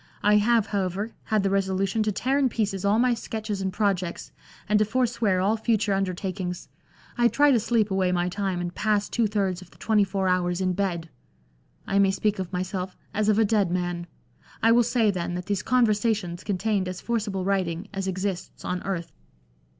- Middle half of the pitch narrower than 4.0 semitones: Yes, average, 2.7 semitones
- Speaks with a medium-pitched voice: No, high, 195 Hz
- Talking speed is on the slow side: No, average, 195 wpm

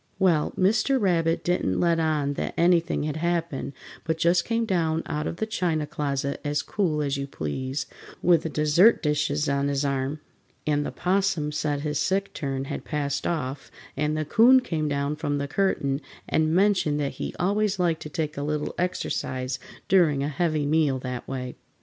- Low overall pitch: No, medium, 155 Hz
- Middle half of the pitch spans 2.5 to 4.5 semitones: Yes, average, 3.6 semitones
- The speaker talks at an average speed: Yes, average, 180 wpm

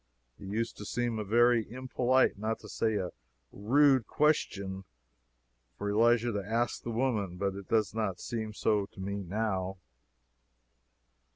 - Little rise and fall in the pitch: No, average, 3.2 semitones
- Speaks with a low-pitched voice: Yes, low, 110 Hz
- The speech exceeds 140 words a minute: Yes, average, 150 wpm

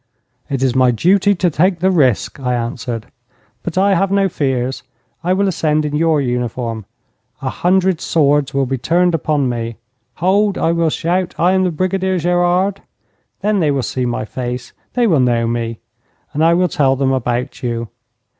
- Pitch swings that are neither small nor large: No, wide, 6.3 semitones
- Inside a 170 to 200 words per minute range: Yes, average, 180 wpm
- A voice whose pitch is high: No, medium, 150 Hz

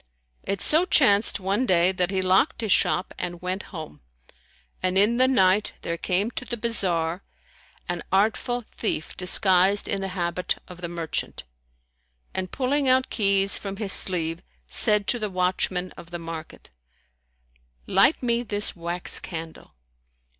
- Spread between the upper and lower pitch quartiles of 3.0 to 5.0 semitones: Yes, average, 3.4 semitones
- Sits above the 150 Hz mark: Yes, high, 190 Hz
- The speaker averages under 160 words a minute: Yes, average, 150 wpm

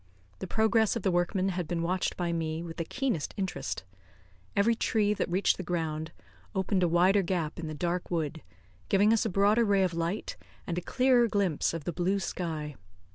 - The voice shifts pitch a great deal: No, average, 3.3 semitones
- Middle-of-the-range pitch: Yes, medium, 180 Hz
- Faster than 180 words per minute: Yes, average, 195 wpm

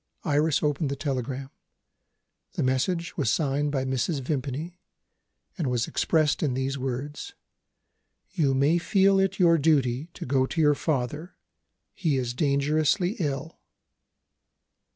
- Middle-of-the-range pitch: Yes, medium, 145 Hz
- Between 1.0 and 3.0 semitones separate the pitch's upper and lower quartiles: No, average, 3.5 semitones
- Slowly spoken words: Yes, slow, 130 wpm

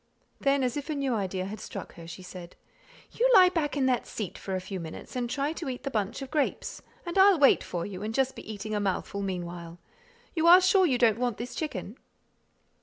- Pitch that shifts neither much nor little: No, wide, 7.1 semitones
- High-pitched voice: Yes, high, 240 Hz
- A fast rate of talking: Yes, fast, 230 wpm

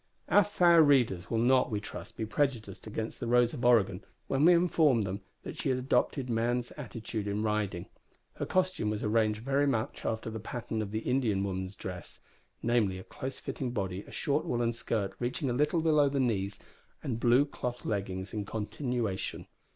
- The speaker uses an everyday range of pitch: Yes, average, 4.2 semitones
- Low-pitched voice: Yes, low, 115 Hz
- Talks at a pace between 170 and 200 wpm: Yes, average, 185 wpm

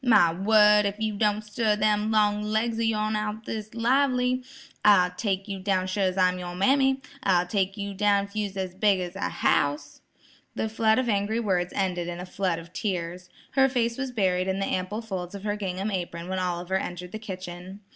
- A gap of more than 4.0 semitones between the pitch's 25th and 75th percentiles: No, average, 2.9 semitones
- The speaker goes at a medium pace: No, fast, 210 wpm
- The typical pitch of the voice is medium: No, high, 200 Hz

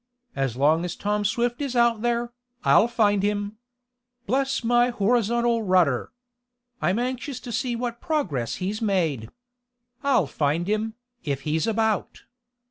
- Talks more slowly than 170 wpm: Yes, slow, 135 wpm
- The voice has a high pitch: Yes, high, 215 Hz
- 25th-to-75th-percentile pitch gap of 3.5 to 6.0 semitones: Yes, average, 5.1 semitones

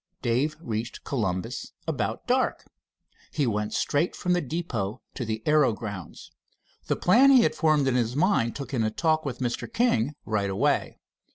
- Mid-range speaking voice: No, low, 130 Hz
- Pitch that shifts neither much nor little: No, wide, 6.2 semitones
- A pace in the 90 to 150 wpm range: No, average, 170 wpm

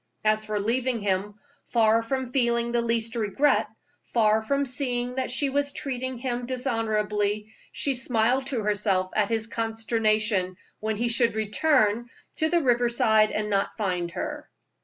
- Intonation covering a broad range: No, average, 2.9 semitones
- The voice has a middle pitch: No, high, 230 Hz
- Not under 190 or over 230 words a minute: No, average, 155 wpm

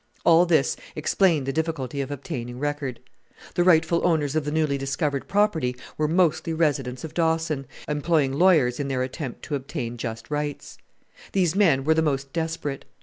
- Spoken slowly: No, average, 165 wpm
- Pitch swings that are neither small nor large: Yes, average, 3.2 semitones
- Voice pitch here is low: No, medium, 150 Hz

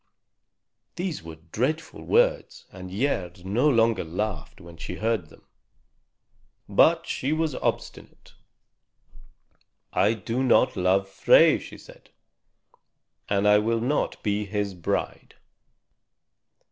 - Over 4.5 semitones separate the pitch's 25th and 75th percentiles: Yes, wide, 5.6 semitones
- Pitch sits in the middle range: No, low, 105 Hz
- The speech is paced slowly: Yes, slow, 110 wpm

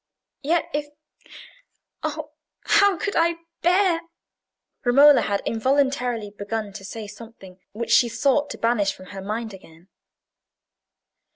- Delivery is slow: Yes, slow, 115 wpm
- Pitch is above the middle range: Yes, high, 245 Hz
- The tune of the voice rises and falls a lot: Yes, wide, 6.3 semitones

